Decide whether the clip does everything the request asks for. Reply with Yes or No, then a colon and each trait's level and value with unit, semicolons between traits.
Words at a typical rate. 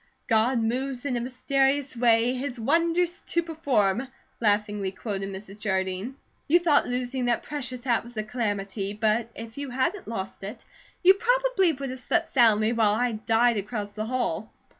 Yes: average, 165 wpm